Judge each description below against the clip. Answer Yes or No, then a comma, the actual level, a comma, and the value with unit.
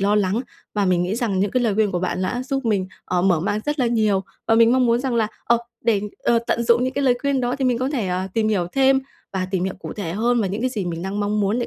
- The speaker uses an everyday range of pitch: Yes, average, 4.2 semitones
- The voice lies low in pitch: No, high, 215 Hz